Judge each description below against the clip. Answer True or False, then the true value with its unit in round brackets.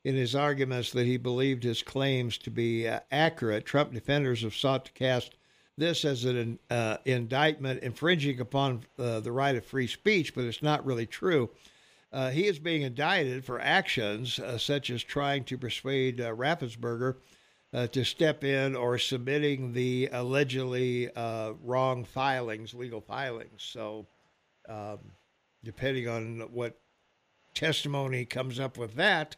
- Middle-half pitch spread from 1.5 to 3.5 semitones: True (2.6 semitones)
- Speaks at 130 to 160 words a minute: True (150 wpm)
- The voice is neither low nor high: False (130 Hz)